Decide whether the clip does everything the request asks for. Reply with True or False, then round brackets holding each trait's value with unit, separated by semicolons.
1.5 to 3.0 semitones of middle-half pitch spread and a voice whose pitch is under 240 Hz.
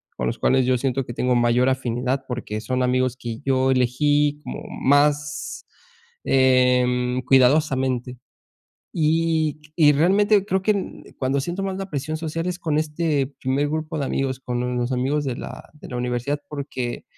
False (3.4 semitones; 135 Hz)